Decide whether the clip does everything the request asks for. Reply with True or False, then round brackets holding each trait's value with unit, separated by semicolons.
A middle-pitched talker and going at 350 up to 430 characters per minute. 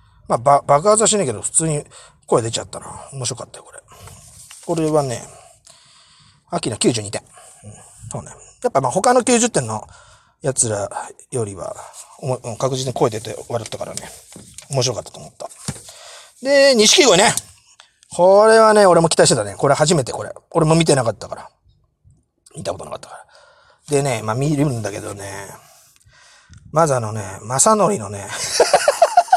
False (150 Hz; 285 characters per minute)